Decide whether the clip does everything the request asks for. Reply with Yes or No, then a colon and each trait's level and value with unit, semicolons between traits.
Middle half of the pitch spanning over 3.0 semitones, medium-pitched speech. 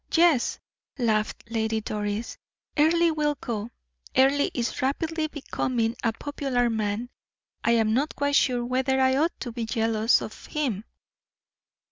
No: average, 4.2 semitones; high, 245 Hz